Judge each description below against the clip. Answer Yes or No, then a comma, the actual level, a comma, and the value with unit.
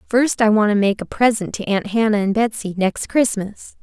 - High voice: Yes, high, 215 Hz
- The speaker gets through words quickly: Yes, fast, 220 wpm